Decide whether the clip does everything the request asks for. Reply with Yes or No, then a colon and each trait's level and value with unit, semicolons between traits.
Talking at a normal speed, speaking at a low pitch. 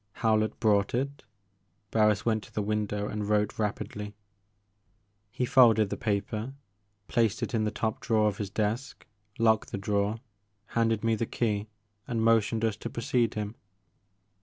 Yes: average, 155 wpm; low, 110 Hz